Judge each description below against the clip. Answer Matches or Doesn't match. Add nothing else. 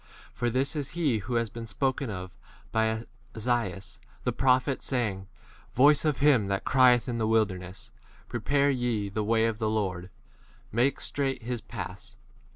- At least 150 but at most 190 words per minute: Matches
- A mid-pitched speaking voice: Doesn't match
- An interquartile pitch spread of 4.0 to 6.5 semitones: Doesn't match